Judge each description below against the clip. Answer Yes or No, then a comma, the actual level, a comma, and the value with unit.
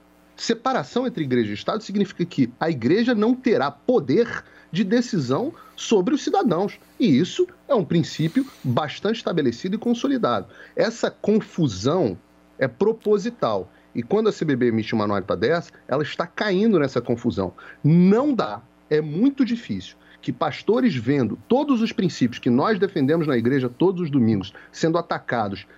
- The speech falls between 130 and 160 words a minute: Yes, average, 150 wpm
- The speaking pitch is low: No, medium, 180 Hz